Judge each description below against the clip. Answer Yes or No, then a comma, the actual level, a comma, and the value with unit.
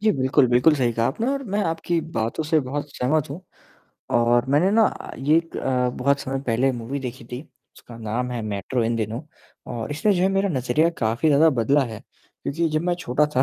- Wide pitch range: No, average, 4.7 semitones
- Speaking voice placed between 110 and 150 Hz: Yes, low, 135 Hz